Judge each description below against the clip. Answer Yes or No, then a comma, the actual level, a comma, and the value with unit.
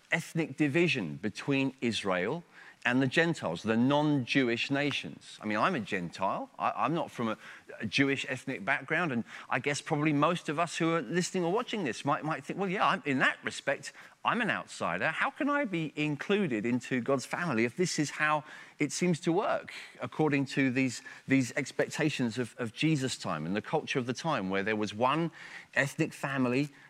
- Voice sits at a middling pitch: Yes, medium, 145 Hz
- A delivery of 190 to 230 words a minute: Yes, average, 195 wpm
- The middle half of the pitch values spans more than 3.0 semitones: Yes, average, 3.9 semitones